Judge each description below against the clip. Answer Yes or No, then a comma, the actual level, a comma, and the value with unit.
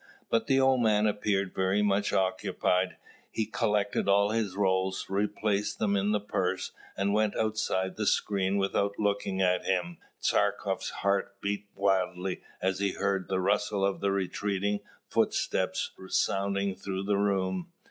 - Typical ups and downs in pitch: No, narrow, 1.5 semitones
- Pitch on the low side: Yes, low, 100 Hz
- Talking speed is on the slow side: No, average, 145 wpm